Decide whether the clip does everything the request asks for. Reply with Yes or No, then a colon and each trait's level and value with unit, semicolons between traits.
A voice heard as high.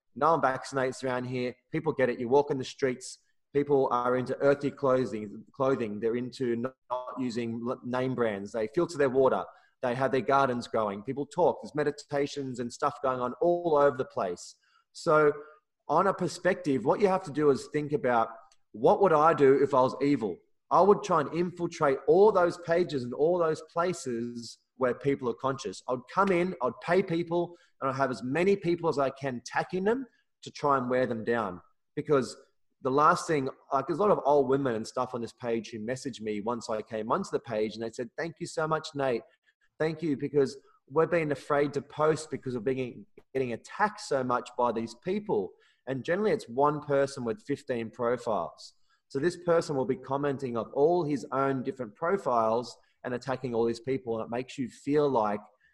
No: low, 135 Hz